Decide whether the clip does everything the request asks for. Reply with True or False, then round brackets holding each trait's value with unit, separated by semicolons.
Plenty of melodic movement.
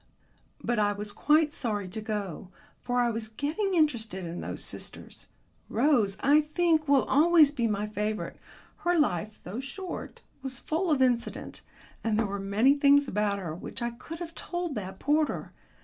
True (6.3 semitones)